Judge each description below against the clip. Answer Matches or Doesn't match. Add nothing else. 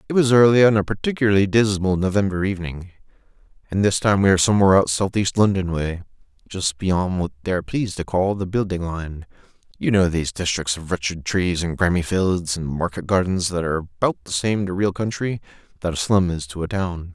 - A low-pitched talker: Matches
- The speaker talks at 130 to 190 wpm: Doesn't match